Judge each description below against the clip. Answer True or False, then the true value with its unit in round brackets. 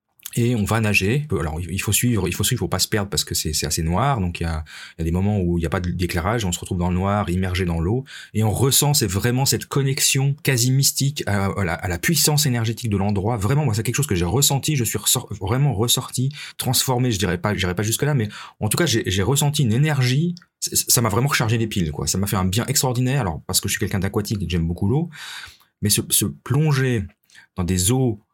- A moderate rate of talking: False (260 wpm)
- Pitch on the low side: True (110 Hz)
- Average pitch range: False (5.9 semitones)